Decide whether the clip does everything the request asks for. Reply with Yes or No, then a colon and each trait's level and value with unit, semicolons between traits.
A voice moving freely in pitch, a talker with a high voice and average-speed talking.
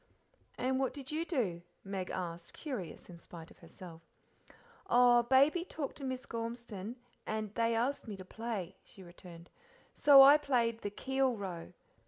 Yes: wide, 6.2 semitones; high, 230 Hz; average, 160 wpm